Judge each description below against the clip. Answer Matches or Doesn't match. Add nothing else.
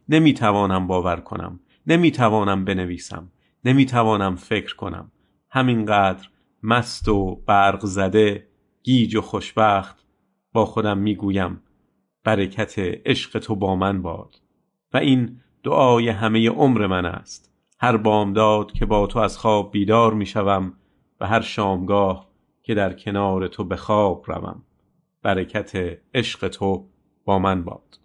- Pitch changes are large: Doesn't match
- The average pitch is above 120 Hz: Doesn't match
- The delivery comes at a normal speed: Matches